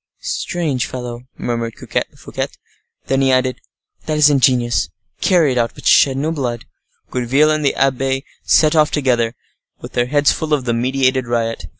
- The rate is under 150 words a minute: No, average, 165 wpm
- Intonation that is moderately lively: Yes, average, 3.2 semitones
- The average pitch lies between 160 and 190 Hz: No, low, 130 Hz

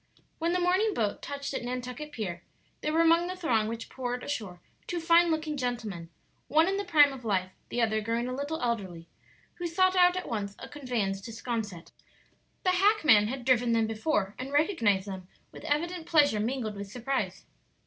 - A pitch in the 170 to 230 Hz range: No, very high, 250 Hz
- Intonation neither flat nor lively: No, wide, 6.9 semitones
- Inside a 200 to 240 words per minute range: No, average, 190 wpm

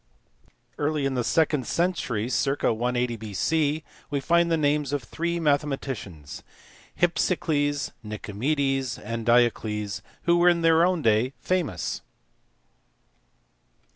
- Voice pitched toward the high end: No, medium, 140 Hz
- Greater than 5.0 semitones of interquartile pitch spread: Yes, wide, 5.5 semitones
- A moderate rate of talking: No, slow, 110 wpm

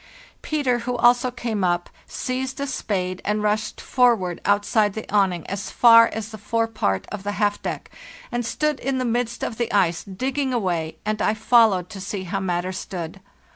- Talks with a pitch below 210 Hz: No, high, 215 Hz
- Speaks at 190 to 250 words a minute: No, average, 180 wpm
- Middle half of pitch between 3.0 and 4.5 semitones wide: Yes, average, 4.2 semitones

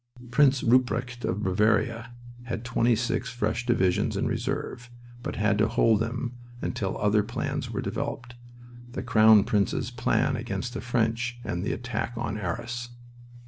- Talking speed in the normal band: Yes, average, 145 wpm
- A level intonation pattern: Yes, narrow, 2.2 semitones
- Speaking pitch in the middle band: No, low, 115 Hz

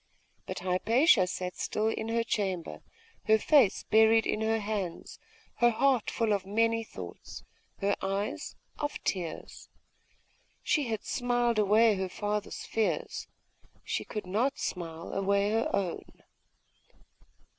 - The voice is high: Yes, high, 215 Hz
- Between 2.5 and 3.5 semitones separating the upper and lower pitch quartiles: Yes, average, 2.9 semitones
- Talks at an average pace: No, slow, 125 wpm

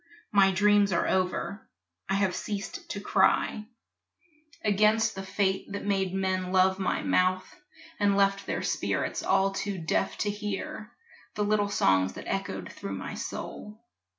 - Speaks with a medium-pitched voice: No, high, 195 Hz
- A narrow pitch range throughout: Yes, narrow, 1.5 semitones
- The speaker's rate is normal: Yes, average, 150 wpm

